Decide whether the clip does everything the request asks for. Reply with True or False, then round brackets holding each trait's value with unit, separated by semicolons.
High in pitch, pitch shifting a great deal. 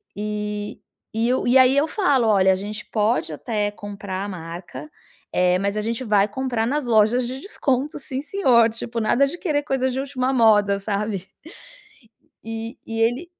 False (225 Hz; 4.1 semitones)